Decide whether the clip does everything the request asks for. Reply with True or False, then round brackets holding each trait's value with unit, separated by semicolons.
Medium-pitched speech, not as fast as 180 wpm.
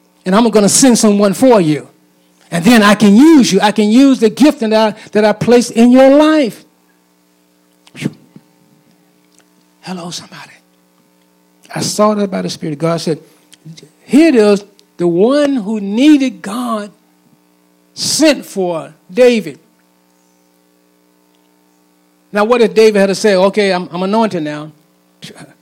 True (175 Hz; 140 wpm)